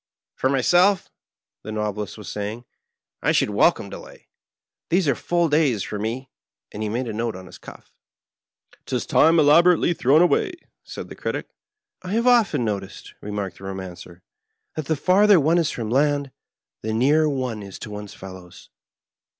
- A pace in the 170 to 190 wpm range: Yes, average, 175 wpm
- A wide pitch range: Yes, wide, 7.6 semitones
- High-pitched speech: No, low, 130 Hz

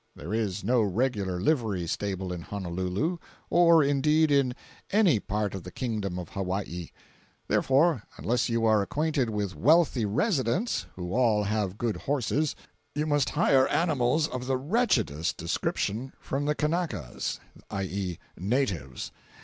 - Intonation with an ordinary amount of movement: No, wide, 7.0 semitones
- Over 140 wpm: No, slow, 135 wpm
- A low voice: Yes, low, 115 Hz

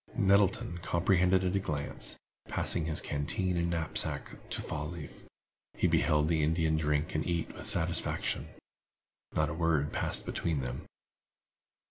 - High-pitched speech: No, very low, 80 Hz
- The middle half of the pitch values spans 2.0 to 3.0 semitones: Yes, average, 2.7 semitones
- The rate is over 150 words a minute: No, average, 145 wpm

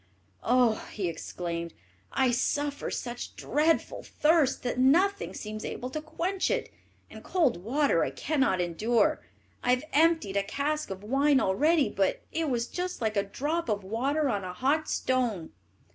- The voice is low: No, very high, 255 Hz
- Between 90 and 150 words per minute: No, average, 160 wpm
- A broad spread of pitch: Yes, wide, 6.4 semitones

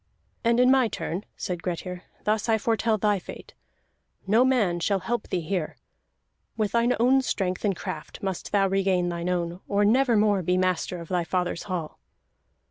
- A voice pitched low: No, high, 195 Hz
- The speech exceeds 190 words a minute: No, average, 175 wpm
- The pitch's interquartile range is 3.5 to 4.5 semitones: Yes, average, 3.8 semitones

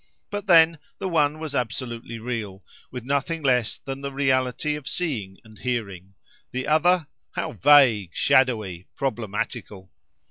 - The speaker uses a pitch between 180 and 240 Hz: No, low, 130 Hz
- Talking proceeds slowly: Yes, slow, 130 wpm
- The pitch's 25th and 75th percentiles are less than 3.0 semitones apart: No, average, 5.2 semitones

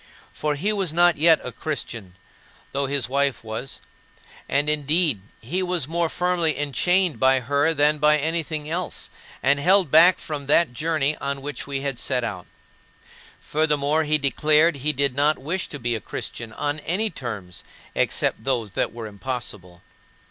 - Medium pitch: Yes, medium, 145 Hz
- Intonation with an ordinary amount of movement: Yes, average, 3.5 semitones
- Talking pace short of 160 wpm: No, average, 165 wpm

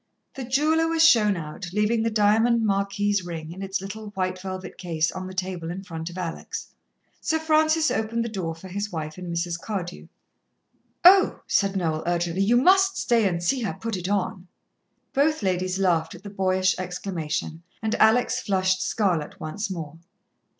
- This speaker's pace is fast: No, average, 175 wpm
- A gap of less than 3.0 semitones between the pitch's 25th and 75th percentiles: No, average, 4.1 semitones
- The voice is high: Yes, high, 195 Hz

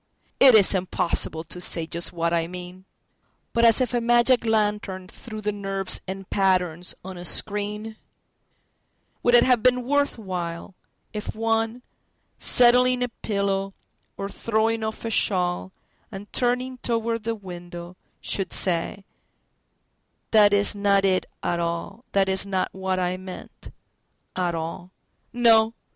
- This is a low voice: No, high, 200 Hz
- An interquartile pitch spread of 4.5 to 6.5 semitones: No, average, 3.7 semitones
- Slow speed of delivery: Yes, slow, 125 wpm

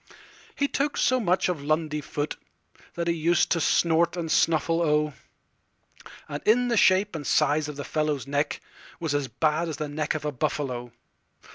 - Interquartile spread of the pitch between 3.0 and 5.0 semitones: No, narrow, 2.6 semitones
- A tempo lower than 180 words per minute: Yes, average, 145 wpm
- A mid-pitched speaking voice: Yes, medium, 155 Hz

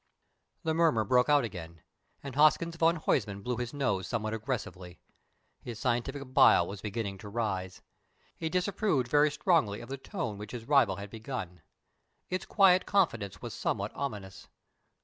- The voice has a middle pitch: No, low, 120 Hz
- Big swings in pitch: Yes, wide, 6.6 semitones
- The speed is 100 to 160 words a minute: Yes, average, 155 wpm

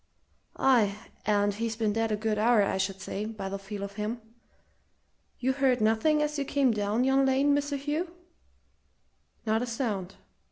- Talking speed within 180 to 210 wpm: No, average, 170 wpm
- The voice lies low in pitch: No, high, 225 Hz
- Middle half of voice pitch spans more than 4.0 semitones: Yes, average, 4.5 semitones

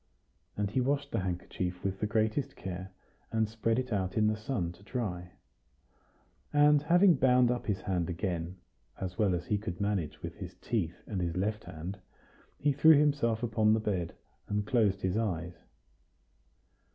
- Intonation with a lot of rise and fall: No, average, 4.7 semitones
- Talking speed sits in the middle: Yes, average, 170 wpm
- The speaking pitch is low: Yes, low, 105 Hz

